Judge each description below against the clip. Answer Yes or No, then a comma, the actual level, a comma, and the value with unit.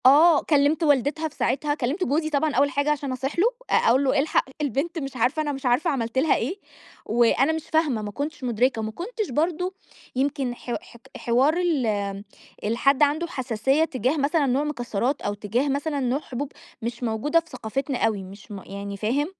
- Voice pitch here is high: Yes, very high, 275 Hz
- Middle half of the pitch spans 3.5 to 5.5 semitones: Yes, average, 4.0 semitones